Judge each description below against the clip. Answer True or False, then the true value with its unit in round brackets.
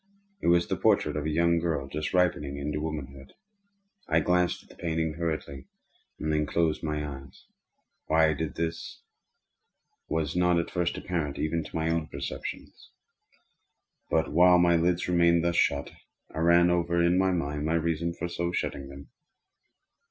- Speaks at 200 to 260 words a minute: False (165 wpm)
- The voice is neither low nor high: False (80 Hz)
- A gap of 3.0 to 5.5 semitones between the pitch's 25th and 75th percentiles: False (2.4 semitones)